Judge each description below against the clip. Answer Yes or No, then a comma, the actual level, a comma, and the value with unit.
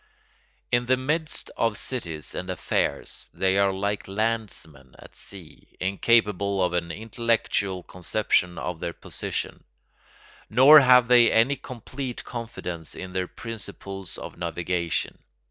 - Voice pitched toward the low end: Yes, low, 100 Hz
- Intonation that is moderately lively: Yes, average, 4.7 semitones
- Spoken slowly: Yes, slow, 125 wpm